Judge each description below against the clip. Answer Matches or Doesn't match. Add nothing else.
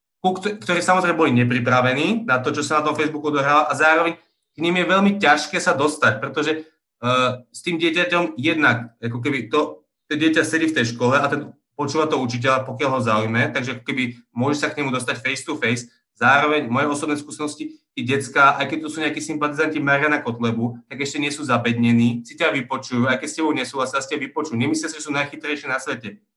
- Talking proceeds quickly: Matches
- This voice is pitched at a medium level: Matches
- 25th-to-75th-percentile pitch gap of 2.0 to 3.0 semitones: Doesn't match